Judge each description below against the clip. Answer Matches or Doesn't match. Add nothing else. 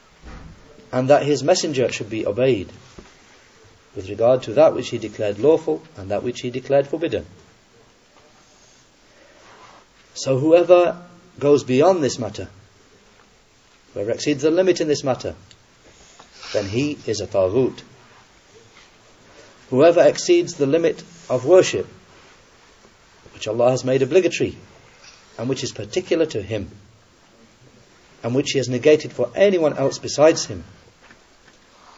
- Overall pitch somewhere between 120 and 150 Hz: Matches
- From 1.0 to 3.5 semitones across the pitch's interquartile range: Doesn't match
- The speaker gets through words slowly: Matches